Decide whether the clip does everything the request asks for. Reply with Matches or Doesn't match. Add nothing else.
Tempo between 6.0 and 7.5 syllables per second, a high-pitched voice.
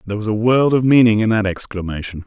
Doesn't match